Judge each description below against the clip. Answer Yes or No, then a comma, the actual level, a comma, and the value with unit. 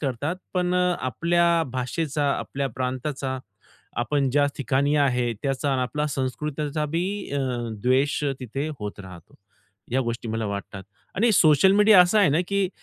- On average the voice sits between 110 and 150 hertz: Yes, medium, 140 Hz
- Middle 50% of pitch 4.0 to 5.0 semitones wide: Yes, average, 4.5 semitones